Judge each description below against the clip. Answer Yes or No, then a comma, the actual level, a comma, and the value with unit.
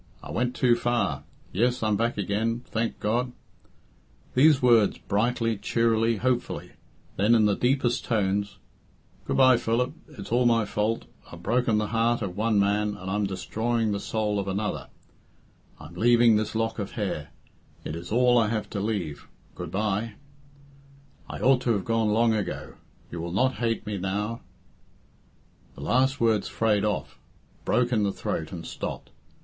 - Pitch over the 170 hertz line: No, low, 110 Hz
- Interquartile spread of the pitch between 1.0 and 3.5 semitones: Yes, average, 2.8 semitones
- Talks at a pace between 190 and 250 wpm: No, average, 170 wpm